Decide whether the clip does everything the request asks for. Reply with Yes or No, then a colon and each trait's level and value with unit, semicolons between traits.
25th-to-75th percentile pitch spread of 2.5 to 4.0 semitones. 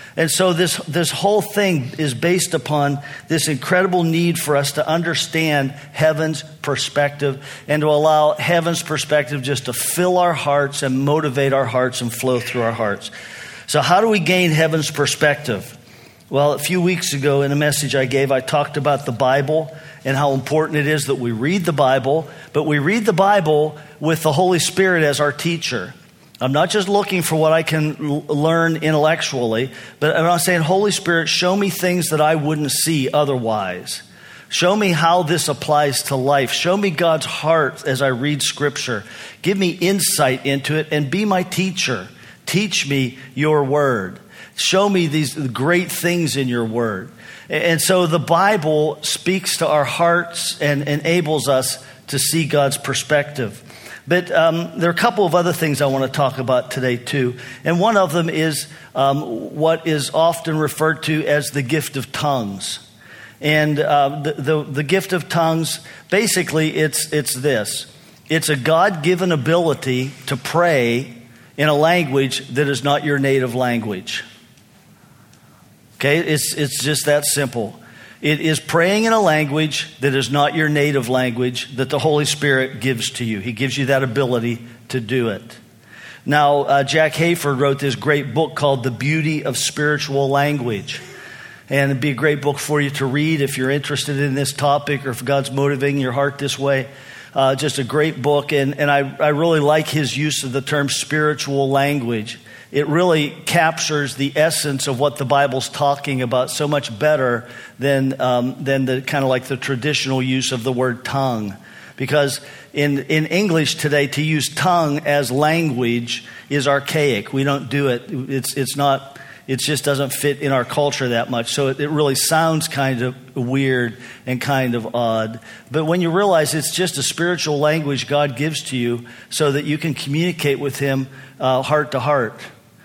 Yes: average, 2.9 semitones